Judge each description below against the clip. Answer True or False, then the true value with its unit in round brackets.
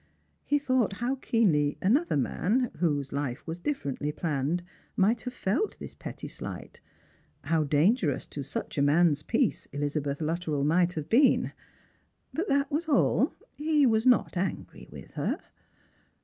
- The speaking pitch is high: False (180 Hz)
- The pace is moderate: True (150 wpm)